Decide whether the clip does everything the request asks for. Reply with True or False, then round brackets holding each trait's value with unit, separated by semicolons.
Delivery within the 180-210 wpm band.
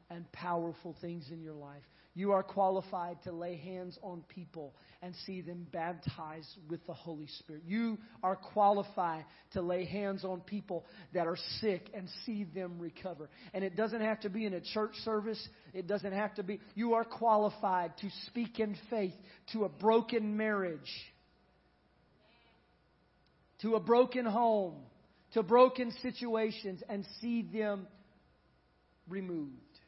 False (150 wpm)